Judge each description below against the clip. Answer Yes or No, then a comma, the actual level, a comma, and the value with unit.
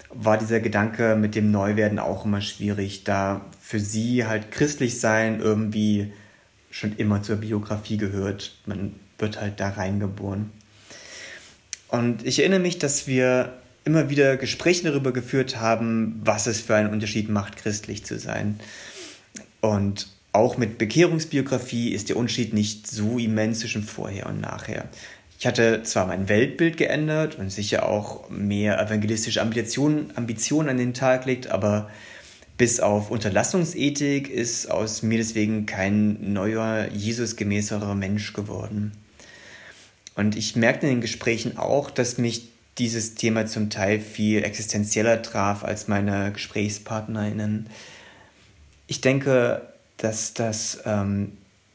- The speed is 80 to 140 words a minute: Yes, average, 130 wpm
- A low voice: Yes, low, 110 Hz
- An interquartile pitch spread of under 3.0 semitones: Yes, narrow, 2.4 semitones